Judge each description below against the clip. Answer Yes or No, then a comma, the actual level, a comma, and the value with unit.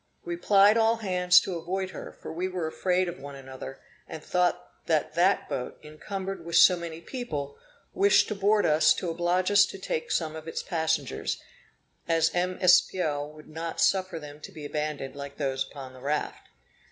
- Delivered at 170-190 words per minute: Yes, average, 185 wpm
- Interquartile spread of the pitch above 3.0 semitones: Yes, average, 3.6 semitones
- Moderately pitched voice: Yes, medium, 170 Hz